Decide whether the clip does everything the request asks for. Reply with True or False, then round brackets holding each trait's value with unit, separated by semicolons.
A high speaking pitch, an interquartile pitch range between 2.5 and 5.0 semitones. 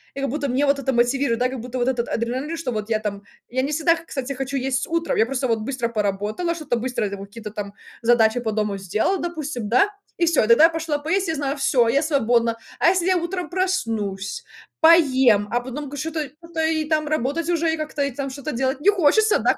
False (270 Hz; 5.4 semitones)